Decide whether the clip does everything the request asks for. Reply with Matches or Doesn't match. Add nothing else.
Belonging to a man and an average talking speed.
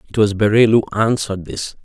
Matches